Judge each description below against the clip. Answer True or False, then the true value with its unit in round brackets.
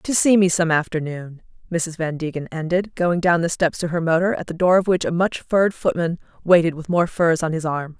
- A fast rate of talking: True (240 wpm)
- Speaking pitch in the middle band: True (170 Hz)